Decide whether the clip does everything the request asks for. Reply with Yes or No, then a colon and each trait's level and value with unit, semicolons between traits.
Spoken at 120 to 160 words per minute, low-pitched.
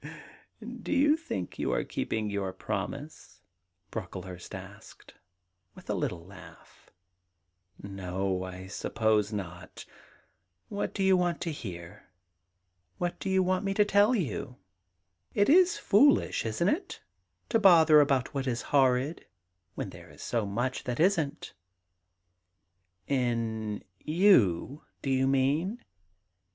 Yes: slow, 135 wpm; low, 120 Hz